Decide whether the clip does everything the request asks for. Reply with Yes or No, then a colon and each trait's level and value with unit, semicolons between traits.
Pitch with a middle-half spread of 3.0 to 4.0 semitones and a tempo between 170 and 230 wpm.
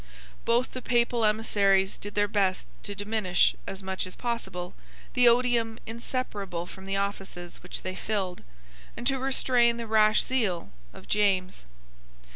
No: average, 3.7 semitones; average, 145 wpm